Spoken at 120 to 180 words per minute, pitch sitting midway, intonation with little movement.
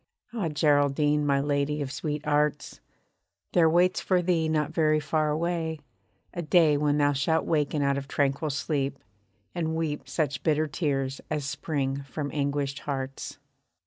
Yes: average, 150 wpm; medium, 150 Hz; narrow, 2.1 semitones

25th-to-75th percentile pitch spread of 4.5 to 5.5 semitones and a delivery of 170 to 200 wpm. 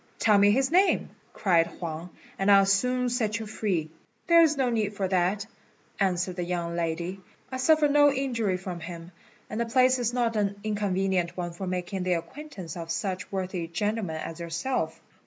Yes: average, 5.0 semitones; average, 180 wpm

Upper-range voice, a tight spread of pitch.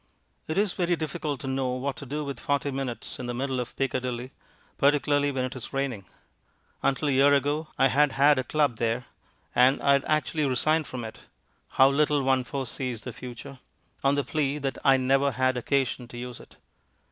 No: low, 135 Hz; narrow, 2.1 semitones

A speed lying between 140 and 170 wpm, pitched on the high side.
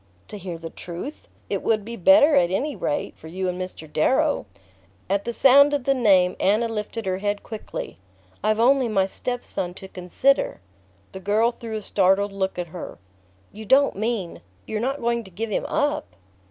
No: average, 190 wpm; high, 215 Hz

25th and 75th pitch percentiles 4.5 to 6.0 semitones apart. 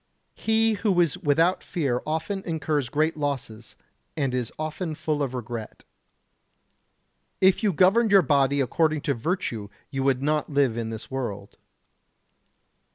Yes: average, 5.1 semitones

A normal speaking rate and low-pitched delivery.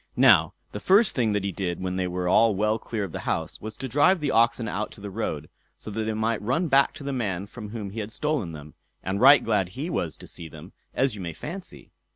No: fast, 255 wpm; low, 110 Hz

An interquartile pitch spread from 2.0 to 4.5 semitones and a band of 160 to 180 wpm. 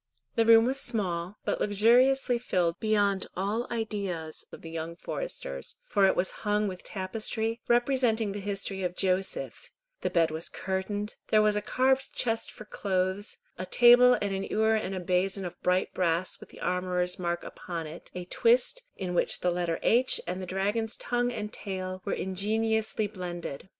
Yes: average, 3.7 semitones; average, 170 wpm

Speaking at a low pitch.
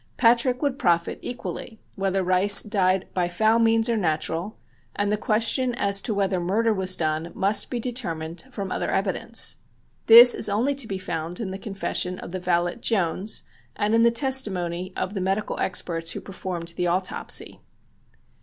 No: high, 195 Hz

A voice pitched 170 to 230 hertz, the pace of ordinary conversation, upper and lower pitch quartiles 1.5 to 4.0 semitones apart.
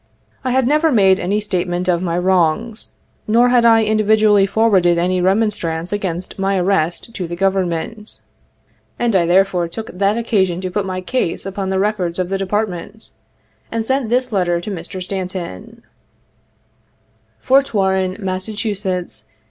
Yes: high, 190 Hz; average, 150 wpm; average, 3.3 semitones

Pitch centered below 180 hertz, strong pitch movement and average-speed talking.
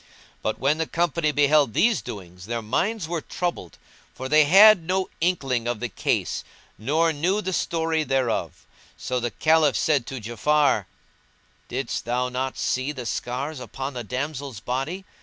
No: medium, 140 Hz; average, 4.7 semitones; average, 160 wpm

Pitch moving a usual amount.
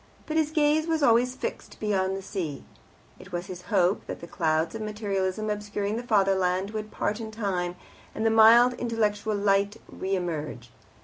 Yes: average, 3.1 semitones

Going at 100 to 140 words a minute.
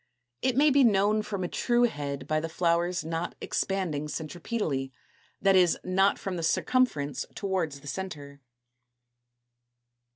Yes: slow, 135 wpm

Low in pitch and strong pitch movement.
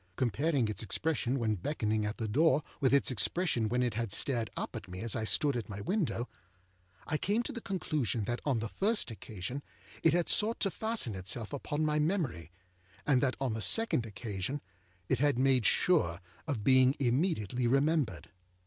Yes: low, 130 Hz; wide, 5.7 semitones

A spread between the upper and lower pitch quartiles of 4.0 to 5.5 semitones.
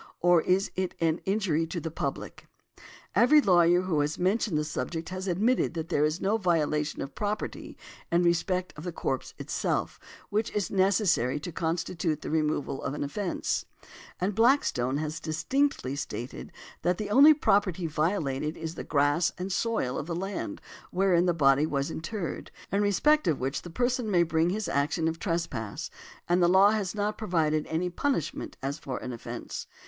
Yes: average, 4.3 semitones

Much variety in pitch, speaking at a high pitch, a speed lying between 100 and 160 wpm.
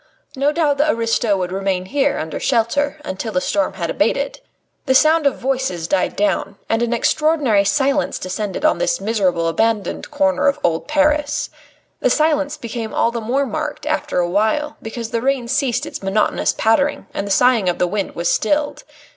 No: wide, 6.3 semitones; high, 240 Hz; average, 185 wpm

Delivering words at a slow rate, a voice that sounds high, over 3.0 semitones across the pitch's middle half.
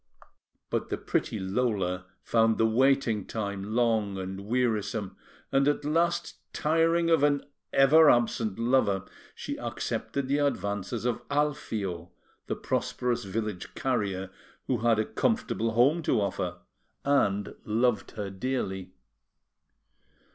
No: slow, 120 wpm; low, 115 Hz; average, 5.3 semitones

